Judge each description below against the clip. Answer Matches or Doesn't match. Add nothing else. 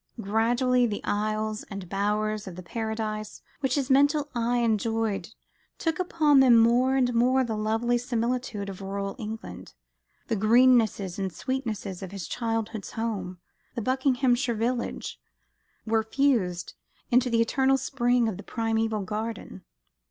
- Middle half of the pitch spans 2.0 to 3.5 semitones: Matches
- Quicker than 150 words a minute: Doesn't match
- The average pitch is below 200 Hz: Doesn't match